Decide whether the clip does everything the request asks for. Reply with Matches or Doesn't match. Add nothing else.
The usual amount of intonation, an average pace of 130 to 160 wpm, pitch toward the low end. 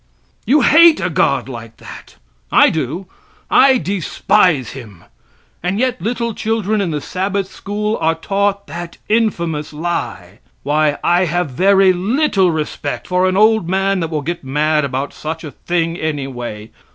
Doesn't match